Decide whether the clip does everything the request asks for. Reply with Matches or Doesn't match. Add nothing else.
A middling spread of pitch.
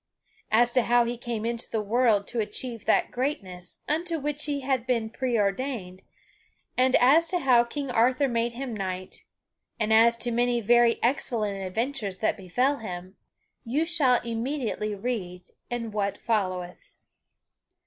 Matches